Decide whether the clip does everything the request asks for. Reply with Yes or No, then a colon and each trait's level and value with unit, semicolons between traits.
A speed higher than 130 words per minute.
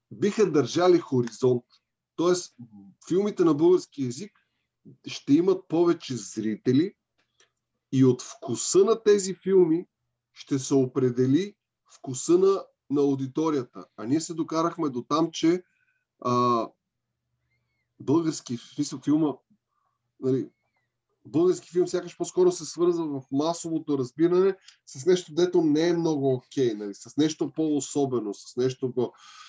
No: average, 120 wpm